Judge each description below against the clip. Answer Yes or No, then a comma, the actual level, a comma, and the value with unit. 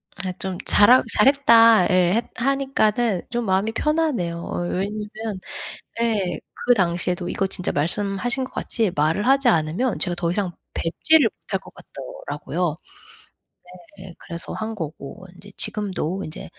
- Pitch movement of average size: Yes, average, 4.8 semitones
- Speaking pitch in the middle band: No, high, 200 Hz